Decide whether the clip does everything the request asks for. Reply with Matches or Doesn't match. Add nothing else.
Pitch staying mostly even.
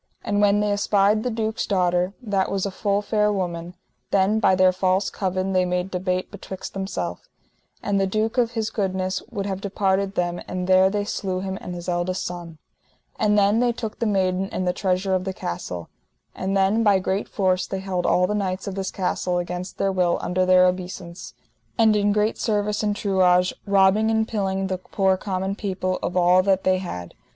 Matches